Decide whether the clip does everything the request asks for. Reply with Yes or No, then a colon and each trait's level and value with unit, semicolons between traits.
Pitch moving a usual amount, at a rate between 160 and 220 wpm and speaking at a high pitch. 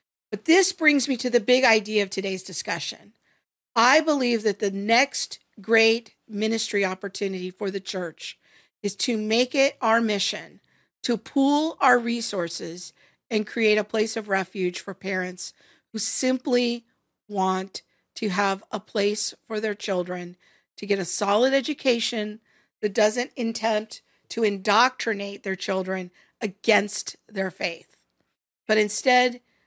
No: average, 3.4 semitones; slow, 135 wpm; high, 215 Hz